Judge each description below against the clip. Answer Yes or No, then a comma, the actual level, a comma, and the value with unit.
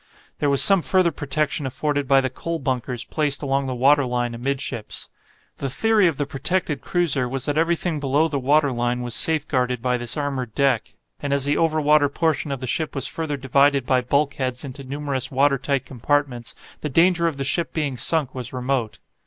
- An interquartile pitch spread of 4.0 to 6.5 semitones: No, average, 2.8 semitones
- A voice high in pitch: No, medium, 140 Hz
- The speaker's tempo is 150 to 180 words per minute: No, average, 200 wpm